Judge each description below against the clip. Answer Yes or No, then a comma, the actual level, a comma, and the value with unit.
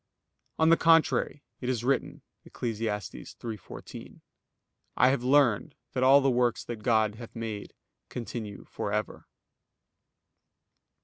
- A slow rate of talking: Yes, slow, 120 wpm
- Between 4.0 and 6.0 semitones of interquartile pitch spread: No, average, 3.4 semitones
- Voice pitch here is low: Yes, low, 120 Hz